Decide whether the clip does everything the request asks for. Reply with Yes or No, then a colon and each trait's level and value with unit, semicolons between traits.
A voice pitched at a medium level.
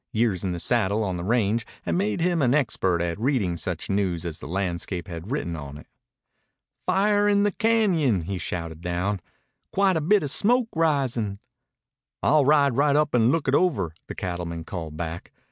No: low, 105 Hz